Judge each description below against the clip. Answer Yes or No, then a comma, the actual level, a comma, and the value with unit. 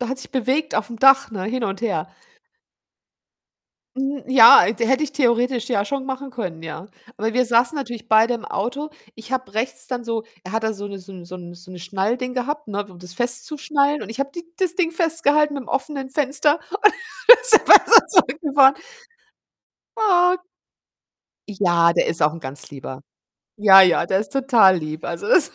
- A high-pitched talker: Yes, high, 240 Hz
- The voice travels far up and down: Yes, wide, 6.1 semitones